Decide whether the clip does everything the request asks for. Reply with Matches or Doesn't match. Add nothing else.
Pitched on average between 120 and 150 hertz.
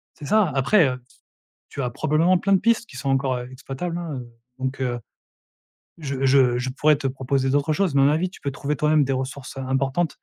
Matches